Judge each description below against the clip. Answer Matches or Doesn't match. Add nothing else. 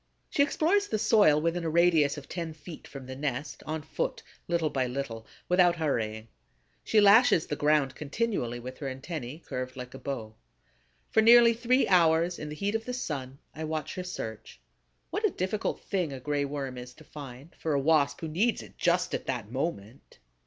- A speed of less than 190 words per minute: Doesn't match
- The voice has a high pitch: Doesn't match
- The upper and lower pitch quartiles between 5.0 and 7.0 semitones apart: Matches